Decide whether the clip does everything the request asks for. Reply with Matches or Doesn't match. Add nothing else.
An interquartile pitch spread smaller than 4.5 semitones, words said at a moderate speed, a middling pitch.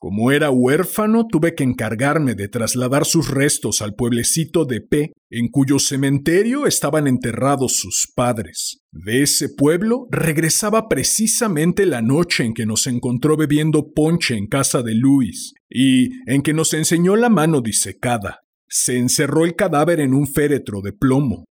Doesn't match